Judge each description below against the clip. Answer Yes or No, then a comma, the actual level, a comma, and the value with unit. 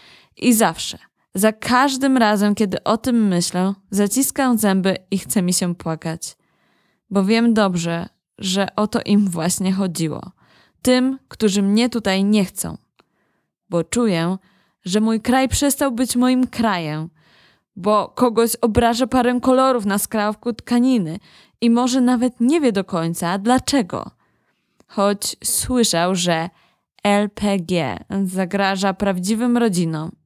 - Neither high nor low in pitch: No, high, 205 Hz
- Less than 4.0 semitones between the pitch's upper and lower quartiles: No, average, 4.4 semitones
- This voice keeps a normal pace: Yes, average, 125 wpm